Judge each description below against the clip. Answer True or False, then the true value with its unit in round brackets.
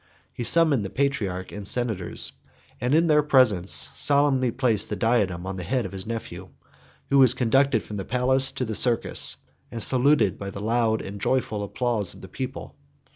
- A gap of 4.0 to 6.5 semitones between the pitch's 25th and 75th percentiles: True (4.6 semitones)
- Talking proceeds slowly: False (180 wpm)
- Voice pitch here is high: False (115 Hz)